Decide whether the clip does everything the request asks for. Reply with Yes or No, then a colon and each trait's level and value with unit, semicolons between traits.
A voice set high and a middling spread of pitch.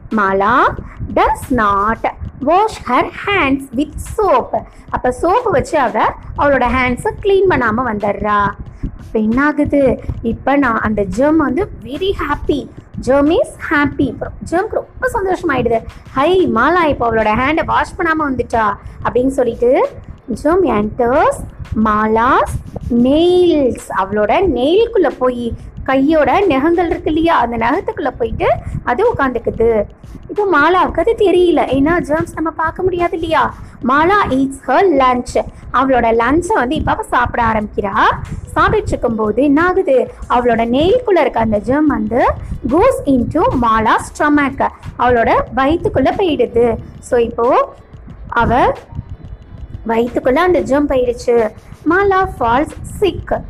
No: very high, 280 Hz; wide, 6.8 semitones